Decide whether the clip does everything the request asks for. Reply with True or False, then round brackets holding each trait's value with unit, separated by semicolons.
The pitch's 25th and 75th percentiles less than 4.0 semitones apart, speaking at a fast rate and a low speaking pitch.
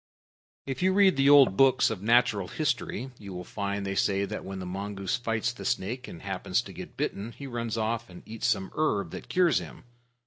False (4.8 semitones; 210 wpm; 115 Hz)